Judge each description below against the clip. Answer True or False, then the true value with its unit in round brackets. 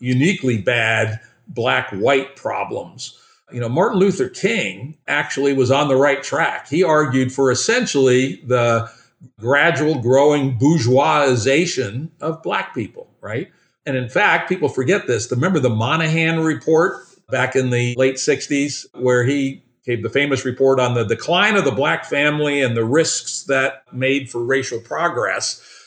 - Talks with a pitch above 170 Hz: False (135 Hz)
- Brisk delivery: False (150 wpm)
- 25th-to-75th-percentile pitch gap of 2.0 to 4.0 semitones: True (3.5 semitones)